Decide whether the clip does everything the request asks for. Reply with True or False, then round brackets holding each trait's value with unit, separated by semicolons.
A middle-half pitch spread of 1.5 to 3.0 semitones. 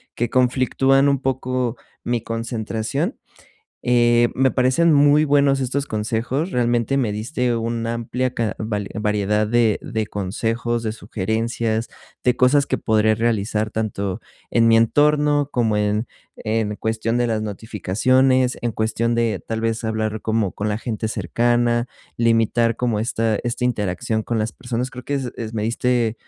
True (2.4 semitones)